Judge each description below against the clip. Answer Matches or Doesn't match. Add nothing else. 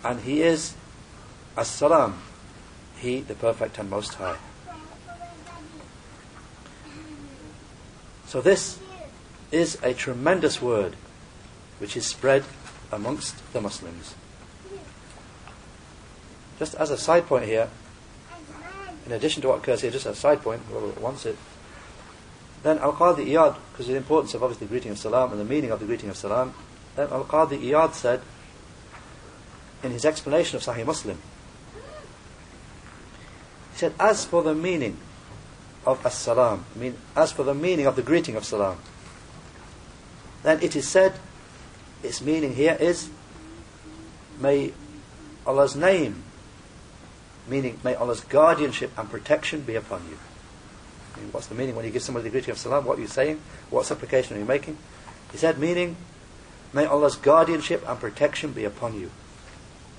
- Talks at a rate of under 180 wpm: Matches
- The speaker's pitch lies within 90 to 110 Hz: Doesn't match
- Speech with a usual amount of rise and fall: Doesn't match